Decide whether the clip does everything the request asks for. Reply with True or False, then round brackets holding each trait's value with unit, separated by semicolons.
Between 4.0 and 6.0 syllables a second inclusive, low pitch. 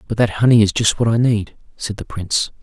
True (5.9 syllables/s; 110 Hz)